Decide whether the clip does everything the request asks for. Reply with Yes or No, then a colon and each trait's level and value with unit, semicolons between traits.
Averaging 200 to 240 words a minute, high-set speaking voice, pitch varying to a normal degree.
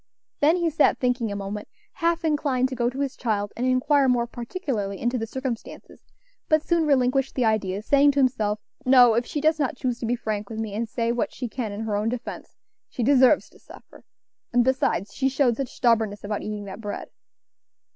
Yes: fast, 205 wpm; high, 245 Hz; average, 3.8 semitones